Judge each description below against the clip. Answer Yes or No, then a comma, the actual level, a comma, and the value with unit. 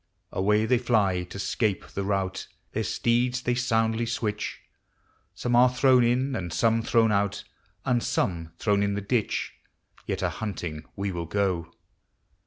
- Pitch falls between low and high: No, low, 105 Hz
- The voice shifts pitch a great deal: No, average, 3.7 semitones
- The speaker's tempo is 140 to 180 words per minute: Yes, average, 155 wpm